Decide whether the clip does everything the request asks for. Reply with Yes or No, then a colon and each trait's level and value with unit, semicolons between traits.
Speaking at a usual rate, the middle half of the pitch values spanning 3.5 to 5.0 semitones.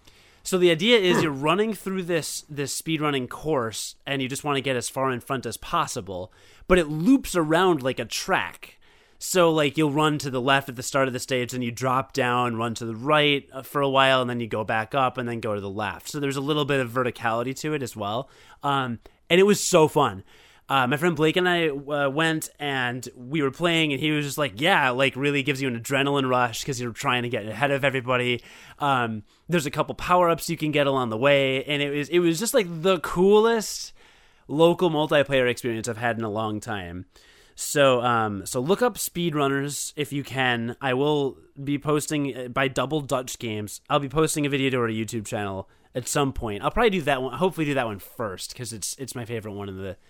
No: fast, 230 wpm; average, 3.9 semitones